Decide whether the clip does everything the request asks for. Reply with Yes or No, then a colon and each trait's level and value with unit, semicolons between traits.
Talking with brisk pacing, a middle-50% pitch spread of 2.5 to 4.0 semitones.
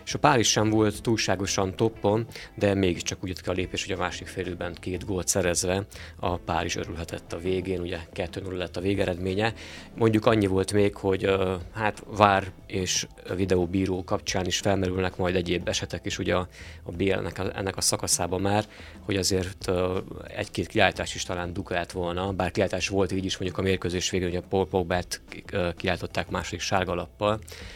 No: fast, 175 wpm; narrow, 1.9 semitones